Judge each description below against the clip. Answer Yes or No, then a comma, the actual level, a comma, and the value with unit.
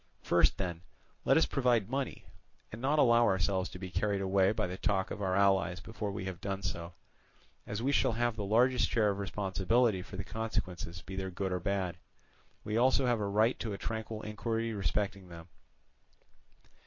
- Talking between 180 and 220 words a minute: Yes, average, 190 wpm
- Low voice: Yes, low, 100 Hz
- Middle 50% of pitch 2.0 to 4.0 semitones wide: Yes, average, 3.2 semitones